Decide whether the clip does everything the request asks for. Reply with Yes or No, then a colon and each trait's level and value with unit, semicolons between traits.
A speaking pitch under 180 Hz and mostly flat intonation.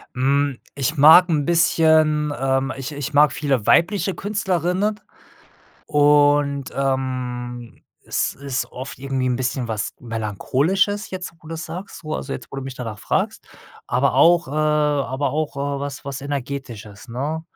No: medium, 140 Hz; average, 3.2 semitones